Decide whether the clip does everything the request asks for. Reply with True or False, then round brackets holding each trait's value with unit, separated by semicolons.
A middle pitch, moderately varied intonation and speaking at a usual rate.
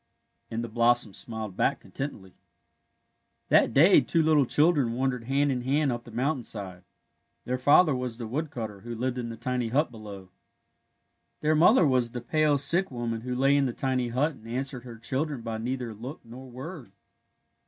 False (125 Hz; 3.4 semitones; 185 wpm)